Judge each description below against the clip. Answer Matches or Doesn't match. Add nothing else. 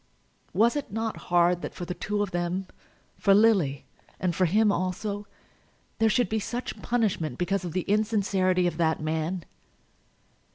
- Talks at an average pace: Matches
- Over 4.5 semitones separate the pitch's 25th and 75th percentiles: Doesn't match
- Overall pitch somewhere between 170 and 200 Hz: Matches